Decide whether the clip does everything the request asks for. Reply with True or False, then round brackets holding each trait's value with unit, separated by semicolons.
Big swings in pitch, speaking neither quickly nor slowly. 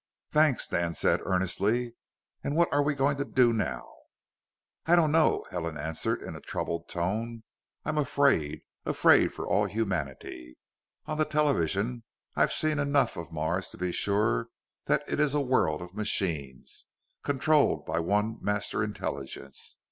True (9.0 semitones; 150 wpm)